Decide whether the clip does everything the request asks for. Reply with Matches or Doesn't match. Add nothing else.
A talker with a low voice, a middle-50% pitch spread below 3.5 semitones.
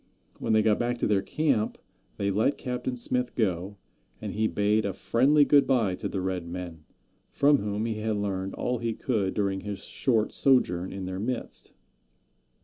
Doesn't match